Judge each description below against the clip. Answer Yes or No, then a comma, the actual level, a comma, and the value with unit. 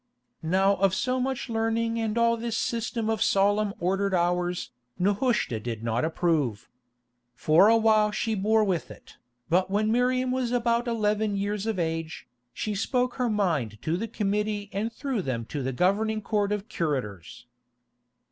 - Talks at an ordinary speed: Yes, average, 160 wpm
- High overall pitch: Yes, high, 205 Hz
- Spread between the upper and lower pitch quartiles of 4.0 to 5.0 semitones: Yes, average, 4.5 semitones